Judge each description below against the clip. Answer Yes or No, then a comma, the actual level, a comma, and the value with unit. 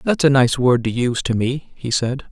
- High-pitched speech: No, low, 130 Hz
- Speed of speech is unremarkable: No, fast, 260 wpm